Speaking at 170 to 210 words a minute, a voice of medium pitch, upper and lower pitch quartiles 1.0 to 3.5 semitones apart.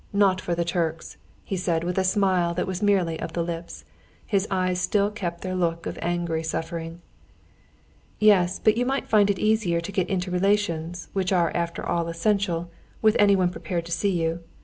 Yes: average, 190 wpm; medium, 180 Hz; average, 2.8 semitones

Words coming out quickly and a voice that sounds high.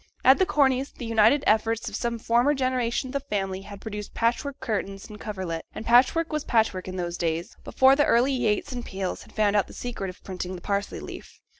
Yes: fast, 215 wpm; high, 225 Hz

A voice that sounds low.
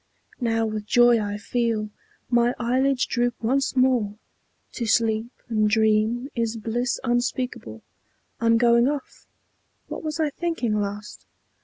No: high, 235 Hz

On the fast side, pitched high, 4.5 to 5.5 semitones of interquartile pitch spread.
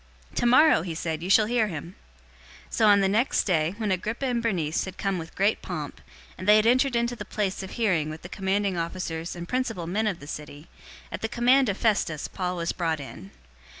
Yes: fast, 215 wpm; high, 195 Hz; average, 4.9 semitones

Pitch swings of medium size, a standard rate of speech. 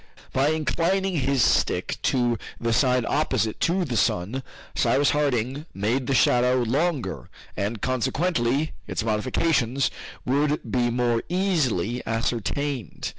No: average, 4.1 semitones; slow, 120 wpm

